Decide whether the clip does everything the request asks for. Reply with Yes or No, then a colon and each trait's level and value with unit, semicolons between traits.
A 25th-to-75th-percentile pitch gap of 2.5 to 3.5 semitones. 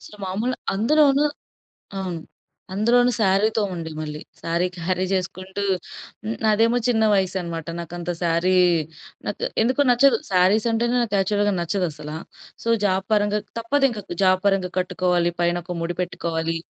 No: average, 4.2 semitones